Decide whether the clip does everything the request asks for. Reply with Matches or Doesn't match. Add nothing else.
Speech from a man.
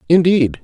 Matches